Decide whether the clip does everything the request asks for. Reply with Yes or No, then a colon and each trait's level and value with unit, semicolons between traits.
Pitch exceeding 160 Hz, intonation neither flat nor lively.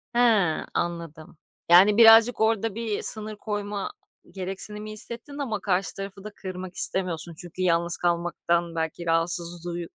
Yes: medium, 185 Hz; average, 3.7 semitones